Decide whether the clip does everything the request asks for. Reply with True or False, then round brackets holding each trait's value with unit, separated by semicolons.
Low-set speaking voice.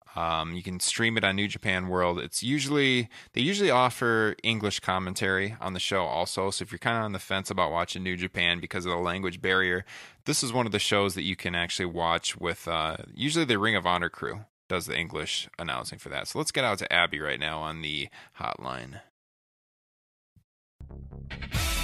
True (95 Hz)